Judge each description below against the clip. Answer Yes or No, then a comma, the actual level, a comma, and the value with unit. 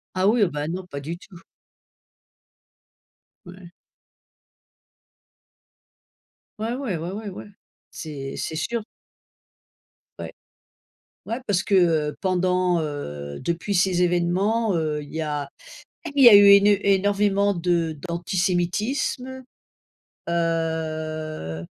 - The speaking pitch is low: No, medium, 175 Hz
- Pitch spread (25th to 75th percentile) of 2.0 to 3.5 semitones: No, average, 4.1 semitones